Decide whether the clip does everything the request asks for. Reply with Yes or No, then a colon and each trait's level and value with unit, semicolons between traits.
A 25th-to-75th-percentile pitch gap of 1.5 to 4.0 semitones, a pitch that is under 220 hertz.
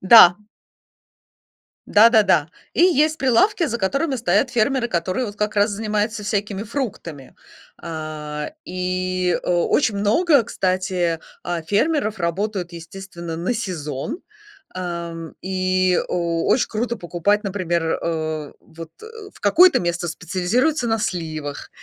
No: average, 4.5 semitones; medium, 185 Hz